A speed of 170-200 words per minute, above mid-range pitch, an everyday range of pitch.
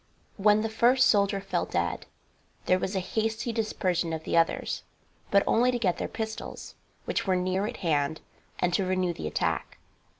Yes: average, 175 wpm; high, 195 Hz; average, 3.6 semitones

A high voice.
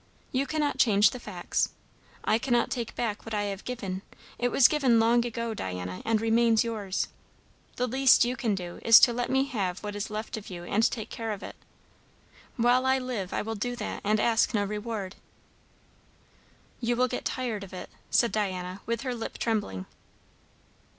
Yes: high, 225 Hz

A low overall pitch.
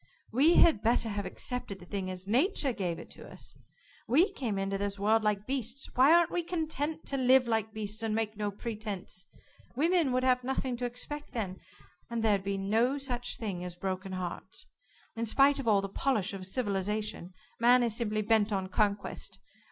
No: high, 220 Hz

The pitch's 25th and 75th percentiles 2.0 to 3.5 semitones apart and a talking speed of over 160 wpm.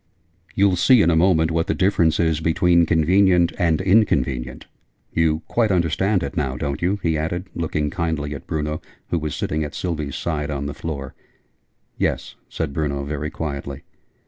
Yes: average, 3.0 semitones; average, 170 wpm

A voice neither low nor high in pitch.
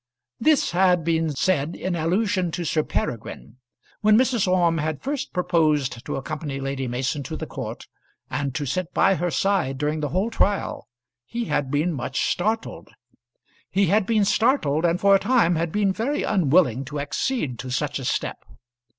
Yes: medium, 170 Hz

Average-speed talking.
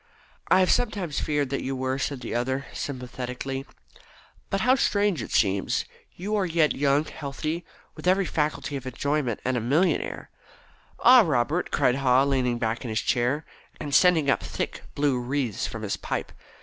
Yes: average, 175 wpm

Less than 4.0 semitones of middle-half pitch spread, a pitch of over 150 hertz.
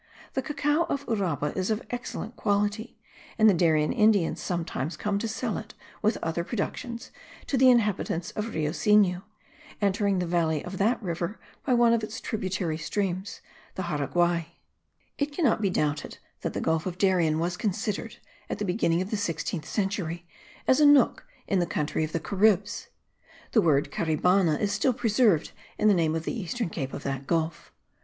No: average, 4.8 semitones; high, 190 Hz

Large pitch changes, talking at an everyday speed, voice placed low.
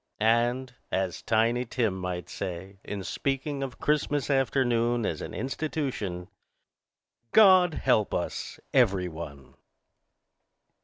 No: wide, 6.1 semitones; slow, 105 wpm; low, 120 Hz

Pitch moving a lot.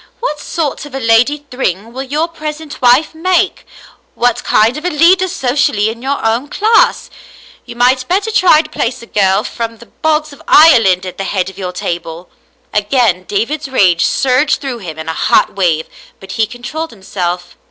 Yes: wide, 7.3 semitones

